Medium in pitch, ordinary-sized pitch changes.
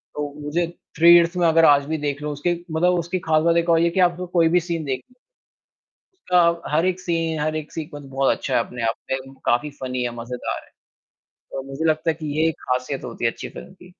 Yes: medium, 155 Hz; average, 3.7 semitones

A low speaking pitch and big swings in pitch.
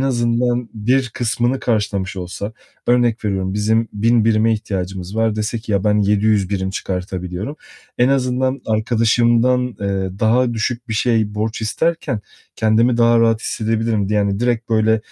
No: low, 110 Hz; narrow, 2.6 semitones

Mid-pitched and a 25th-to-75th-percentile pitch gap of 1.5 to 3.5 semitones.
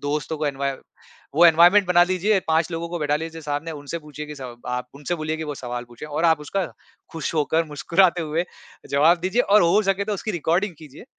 Yes: medium, 160 Hz; average, 2.9 semitones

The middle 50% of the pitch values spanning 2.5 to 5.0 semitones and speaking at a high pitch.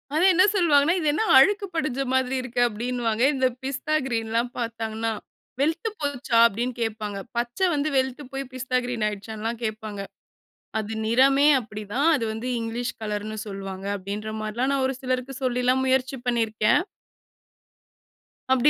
Yes: average, 3.4 semitones; high, 245 Hz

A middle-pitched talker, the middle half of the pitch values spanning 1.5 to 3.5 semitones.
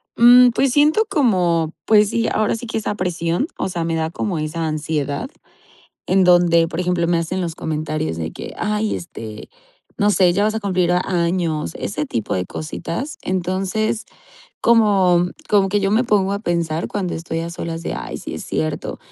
No: medium, 180 Hz; average, 4.1 semitones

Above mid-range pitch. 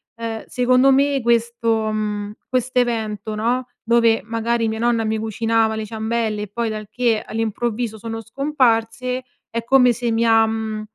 Yes: high, 230 Hz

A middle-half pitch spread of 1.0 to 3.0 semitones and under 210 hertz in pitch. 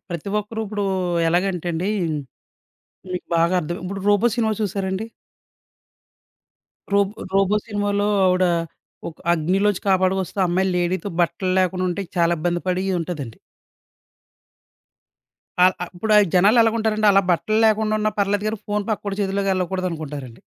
Yes: average, 2.7 semitones; high, 190 Hz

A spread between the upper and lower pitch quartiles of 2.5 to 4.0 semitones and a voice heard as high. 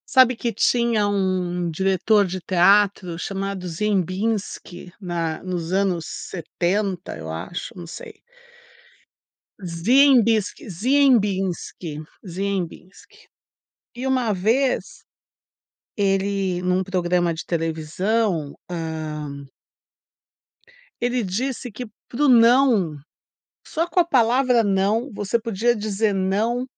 No: average, 4.5 semitones; high, 195 Hz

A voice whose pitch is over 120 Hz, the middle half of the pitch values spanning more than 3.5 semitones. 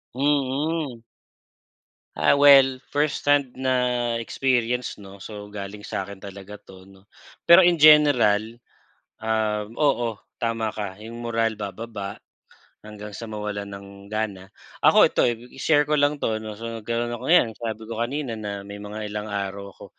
No: low, 115 Hz; average, 4.0 semitones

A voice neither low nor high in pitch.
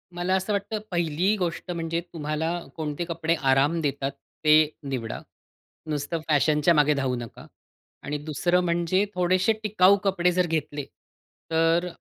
Yes: medium, 165 Hz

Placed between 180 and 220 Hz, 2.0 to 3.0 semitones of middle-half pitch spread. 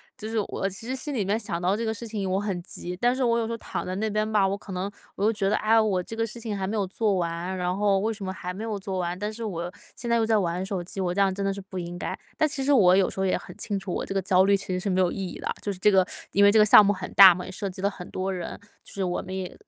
Yes: high, 195 Hz; narrow, 2.6 semitones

